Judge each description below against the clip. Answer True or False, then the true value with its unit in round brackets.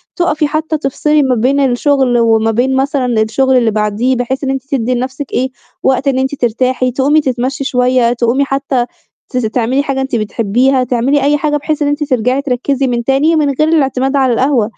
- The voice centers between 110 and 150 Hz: False (265 Hz)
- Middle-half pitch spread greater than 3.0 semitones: False (2.4 semitones)